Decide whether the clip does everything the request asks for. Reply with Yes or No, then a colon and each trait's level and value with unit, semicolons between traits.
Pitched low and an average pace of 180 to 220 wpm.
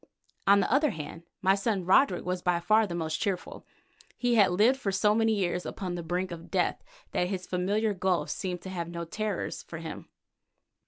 No: medium, 185 Hz; average, 200 wpm